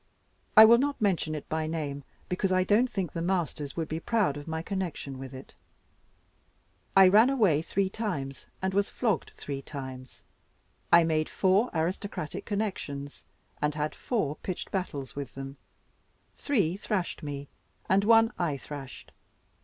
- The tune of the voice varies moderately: No, wide, 5.7 semitones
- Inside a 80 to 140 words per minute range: No, average, 155 wpm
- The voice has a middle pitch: Yes, medium, 170 Hz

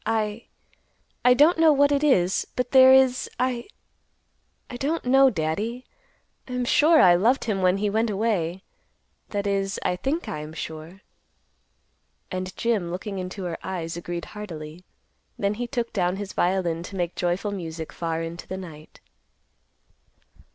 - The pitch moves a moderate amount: No, wide, 5.9 semitones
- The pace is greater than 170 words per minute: No, average, 150 wpm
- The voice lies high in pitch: Yes, high, 195 Hz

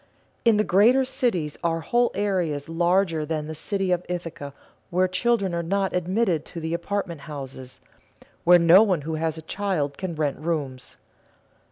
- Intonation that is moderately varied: Yes, average, 3.8 semitones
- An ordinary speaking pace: Yes, average, 165 wpm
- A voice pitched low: No, medium, 170 Hz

